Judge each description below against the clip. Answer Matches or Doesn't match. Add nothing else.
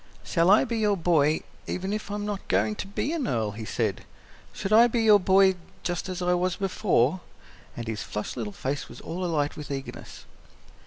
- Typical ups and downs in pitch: Doesn't match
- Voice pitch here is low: Doesn't match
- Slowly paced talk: Doesn't match